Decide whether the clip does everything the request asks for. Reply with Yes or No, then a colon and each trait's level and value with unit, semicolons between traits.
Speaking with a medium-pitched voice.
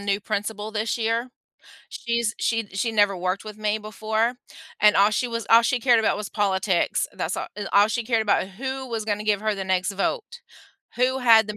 No: high, 215 Hz